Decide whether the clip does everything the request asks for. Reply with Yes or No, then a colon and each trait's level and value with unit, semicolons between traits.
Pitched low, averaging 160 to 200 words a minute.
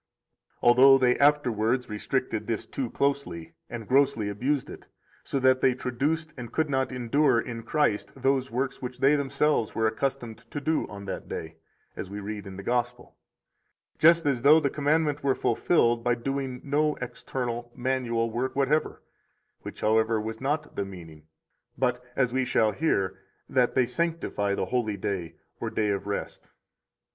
Yes: low, 125 Hz; average, 165 wpm